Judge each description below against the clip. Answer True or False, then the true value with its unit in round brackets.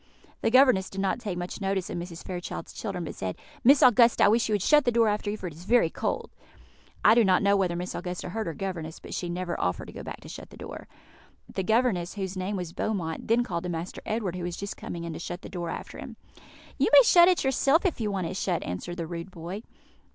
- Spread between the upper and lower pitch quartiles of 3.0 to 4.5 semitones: True (4.1 semitones)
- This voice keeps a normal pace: False (255 wpm)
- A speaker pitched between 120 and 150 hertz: False (190 Hz)